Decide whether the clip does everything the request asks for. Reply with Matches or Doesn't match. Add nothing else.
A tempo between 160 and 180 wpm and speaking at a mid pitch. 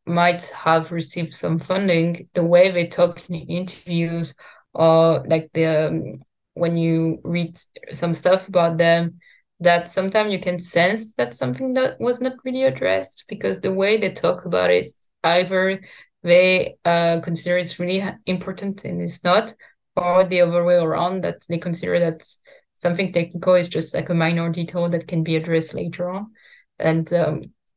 Matches